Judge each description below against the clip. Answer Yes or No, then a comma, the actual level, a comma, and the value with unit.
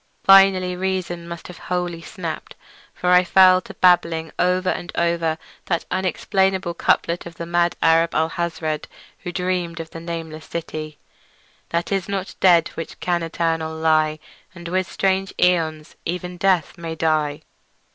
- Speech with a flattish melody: Yes, narrow, 1.9 semitones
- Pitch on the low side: No, medium, 170 Hz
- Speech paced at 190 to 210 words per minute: No, average, 145 wpm